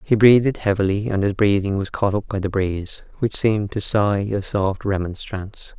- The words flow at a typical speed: Yes, average, 195 wpm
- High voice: No, low, 100 Hz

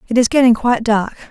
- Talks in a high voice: Yes, high, 235 Hz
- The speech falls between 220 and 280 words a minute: Yes, fast, 230 wpm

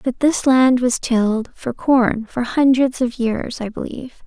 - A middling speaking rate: Yes, average, 185 wpm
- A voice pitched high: Yes, very high, 250 Hz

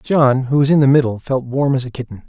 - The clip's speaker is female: No, male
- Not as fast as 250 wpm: No, fast, 290 wpm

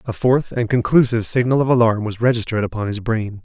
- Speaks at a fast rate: Yes, fast, 210 wpm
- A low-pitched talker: Yes, low, 115 Hz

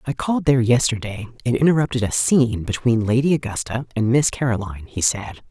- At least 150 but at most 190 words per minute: Yes, average, 175 wpm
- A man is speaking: No, female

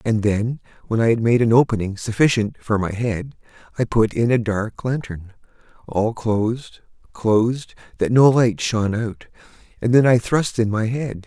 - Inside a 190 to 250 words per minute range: No, average, 175 wpm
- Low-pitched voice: Yes, low, 115 Hz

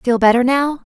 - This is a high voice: Yes, very high, 255 Hz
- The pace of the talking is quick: No, average, 190 wpm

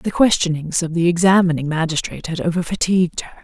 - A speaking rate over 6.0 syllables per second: Yes, 6.3 syllables/s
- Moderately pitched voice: Yes, medium, 170 Hz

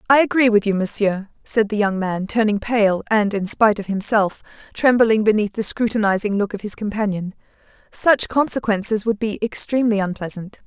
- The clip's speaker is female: Yes, female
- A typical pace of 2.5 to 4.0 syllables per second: No, 5.4 syllables/s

